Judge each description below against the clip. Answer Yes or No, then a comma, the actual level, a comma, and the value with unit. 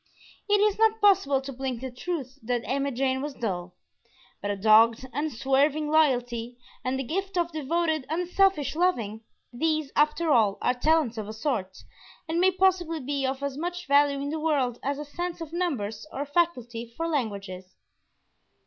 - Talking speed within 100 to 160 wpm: No, average, 175 wpm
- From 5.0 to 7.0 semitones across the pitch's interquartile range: Yes, average, 5.3 semitones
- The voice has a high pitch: Yes, very high, 280 Hz